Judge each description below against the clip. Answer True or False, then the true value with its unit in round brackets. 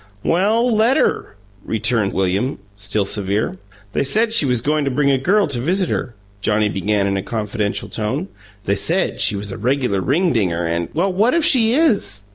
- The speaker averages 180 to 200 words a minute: True (190 wpm)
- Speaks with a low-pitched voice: True (125 Hz)